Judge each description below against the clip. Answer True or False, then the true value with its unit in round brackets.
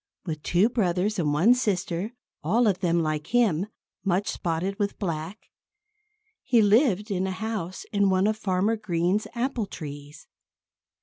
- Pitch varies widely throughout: False (4.0 semitones)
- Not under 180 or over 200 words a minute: False (145 wpm)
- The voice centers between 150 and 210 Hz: True (190 Hz)